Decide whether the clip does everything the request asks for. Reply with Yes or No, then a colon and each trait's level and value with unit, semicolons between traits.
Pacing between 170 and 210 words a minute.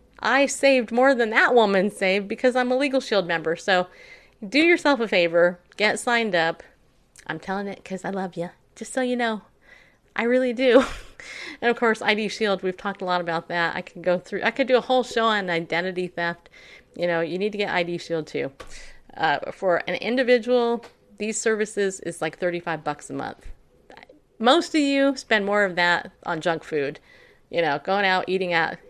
Yes: average, 200 wpm